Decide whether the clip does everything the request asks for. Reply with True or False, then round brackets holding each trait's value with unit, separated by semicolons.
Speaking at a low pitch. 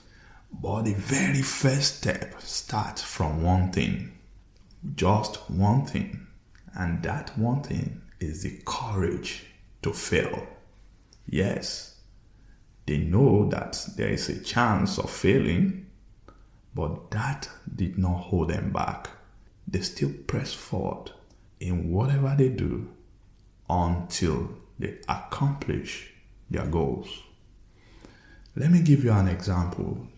True (100 Hz)